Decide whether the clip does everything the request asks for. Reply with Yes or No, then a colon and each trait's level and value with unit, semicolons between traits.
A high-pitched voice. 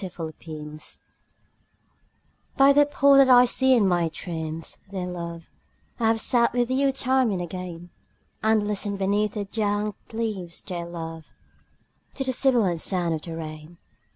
Yes: high, 200 Hz